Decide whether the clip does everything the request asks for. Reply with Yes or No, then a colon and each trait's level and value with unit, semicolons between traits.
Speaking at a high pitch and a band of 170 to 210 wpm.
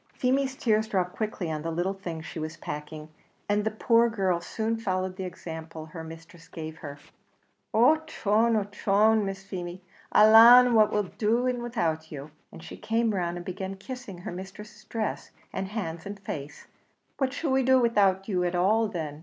Yes: high, 195 Hz; average, 180 wpm